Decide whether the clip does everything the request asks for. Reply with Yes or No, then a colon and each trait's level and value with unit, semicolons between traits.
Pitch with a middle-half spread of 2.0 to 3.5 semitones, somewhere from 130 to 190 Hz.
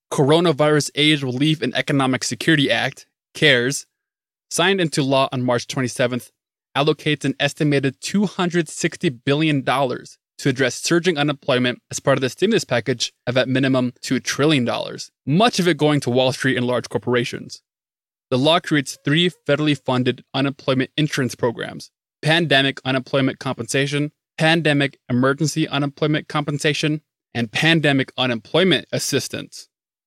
Yes: average, 3.1 semitones; medium, 140 Hz